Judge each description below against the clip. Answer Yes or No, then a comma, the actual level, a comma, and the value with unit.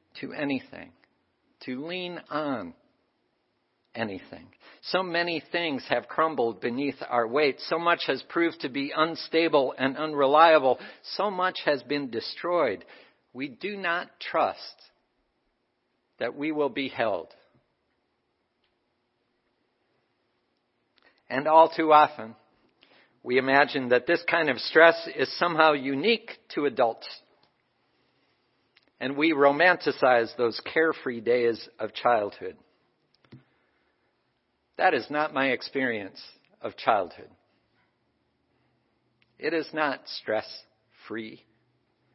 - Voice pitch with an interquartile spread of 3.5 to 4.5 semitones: No, average, 5.3 semitones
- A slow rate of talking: Yes, slow, 105 wpm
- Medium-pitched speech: Yes, medium, 145 Hz